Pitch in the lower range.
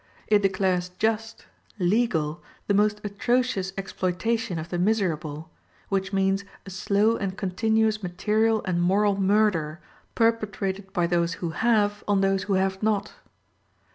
No: high, 195 Hz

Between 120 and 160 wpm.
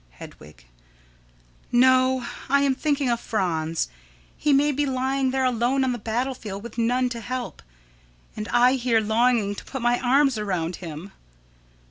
Yes: average, 155 wpm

